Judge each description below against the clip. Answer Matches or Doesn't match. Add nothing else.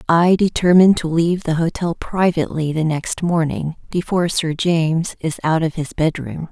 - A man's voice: Doesn't match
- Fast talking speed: Doesn't match